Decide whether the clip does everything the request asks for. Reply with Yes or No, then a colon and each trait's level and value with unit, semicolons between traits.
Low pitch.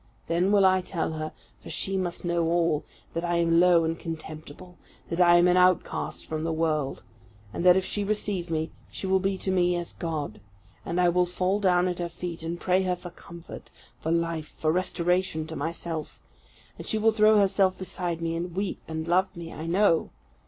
No: medium, 175 Hz